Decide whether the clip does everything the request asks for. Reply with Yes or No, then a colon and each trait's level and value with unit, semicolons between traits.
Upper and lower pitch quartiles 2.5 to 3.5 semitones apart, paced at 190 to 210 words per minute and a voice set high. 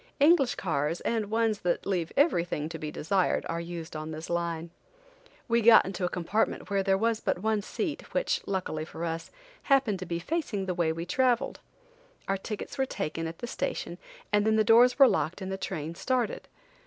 No: average, 5.3 semitones; average, 195 wpm; high, 195 Hz